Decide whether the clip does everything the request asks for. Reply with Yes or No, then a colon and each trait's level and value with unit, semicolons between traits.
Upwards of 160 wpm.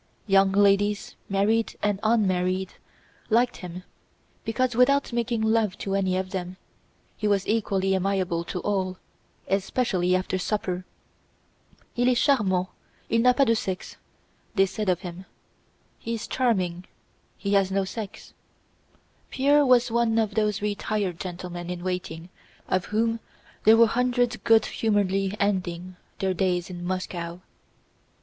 No: average, 140 wpm